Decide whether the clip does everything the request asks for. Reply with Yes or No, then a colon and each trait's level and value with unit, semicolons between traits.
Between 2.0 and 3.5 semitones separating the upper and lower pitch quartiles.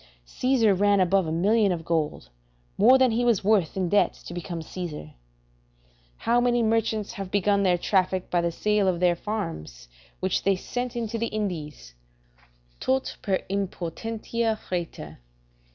No: average, 4.3 semitones